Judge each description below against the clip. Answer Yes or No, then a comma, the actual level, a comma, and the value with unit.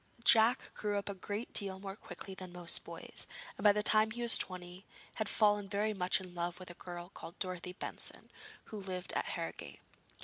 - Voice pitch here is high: Yes, high, 195 Hz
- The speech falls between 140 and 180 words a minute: No, average, 200 wpm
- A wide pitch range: No, narrow, 2.6 semitones